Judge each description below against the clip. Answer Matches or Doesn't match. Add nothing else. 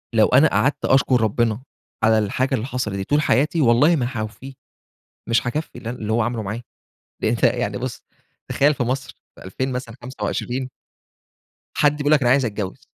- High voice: Doesn't match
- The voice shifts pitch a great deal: Doesn't match